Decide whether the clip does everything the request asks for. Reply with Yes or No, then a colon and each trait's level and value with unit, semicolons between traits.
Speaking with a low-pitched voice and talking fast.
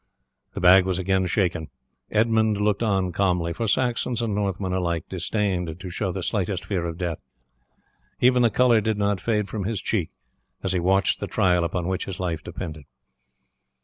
No: very low, 95 Hz; average, 180 wpm